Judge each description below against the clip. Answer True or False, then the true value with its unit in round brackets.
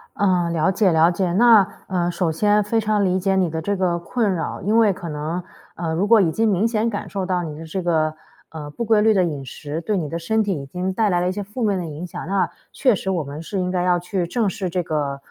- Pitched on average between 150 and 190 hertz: True (185 Hz)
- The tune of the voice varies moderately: True (3.7 semitones)